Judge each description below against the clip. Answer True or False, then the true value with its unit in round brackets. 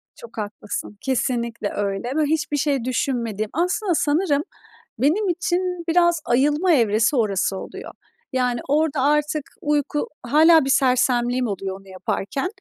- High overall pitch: True (270 Hz)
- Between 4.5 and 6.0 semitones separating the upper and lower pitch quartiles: True (5.1 semitones)